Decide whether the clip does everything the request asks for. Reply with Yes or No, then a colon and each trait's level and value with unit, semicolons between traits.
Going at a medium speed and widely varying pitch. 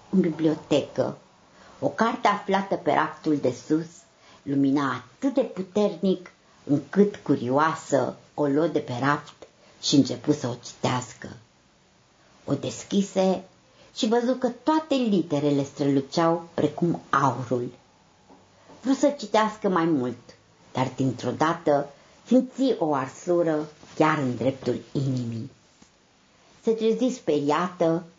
No: slow, 110 wpm; wide, 5.8 semitones